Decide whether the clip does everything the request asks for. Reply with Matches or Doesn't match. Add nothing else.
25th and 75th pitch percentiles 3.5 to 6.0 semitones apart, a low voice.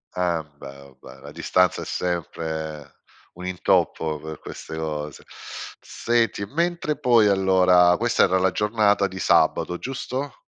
Matches